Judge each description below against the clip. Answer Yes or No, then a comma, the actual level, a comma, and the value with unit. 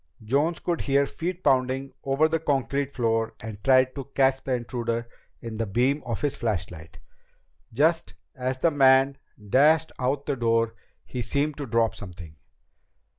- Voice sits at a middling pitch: No, low, 130 Hz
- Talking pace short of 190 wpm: Yes, average, 155 wpm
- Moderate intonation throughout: Yes, average, 3.5 semitones